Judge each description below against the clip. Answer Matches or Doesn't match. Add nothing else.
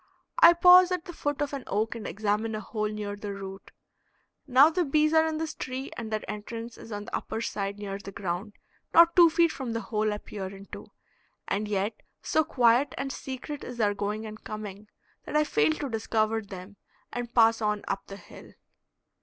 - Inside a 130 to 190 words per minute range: Doesn't match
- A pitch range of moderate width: Doesn't match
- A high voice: Matches